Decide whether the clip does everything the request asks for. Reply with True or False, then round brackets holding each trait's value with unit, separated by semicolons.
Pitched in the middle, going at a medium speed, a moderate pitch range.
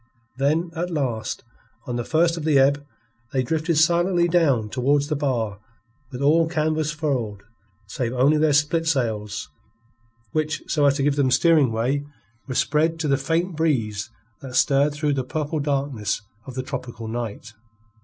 True (145 Hz; 160 wpm; 3.9 semitones)